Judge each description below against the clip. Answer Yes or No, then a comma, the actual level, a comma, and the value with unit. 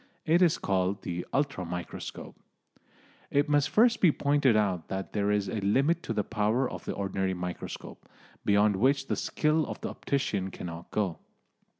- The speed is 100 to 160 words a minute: No, average, 170 wpm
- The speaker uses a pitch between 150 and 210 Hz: No, low, 105 Hz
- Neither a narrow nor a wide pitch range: No, wide, 6.8 semitones